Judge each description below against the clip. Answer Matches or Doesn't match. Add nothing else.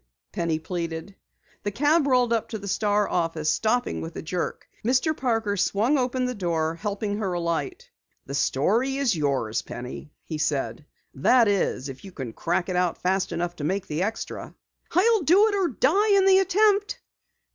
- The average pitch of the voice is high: Matches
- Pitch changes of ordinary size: Doesn't match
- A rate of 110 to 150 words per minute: Doesn't match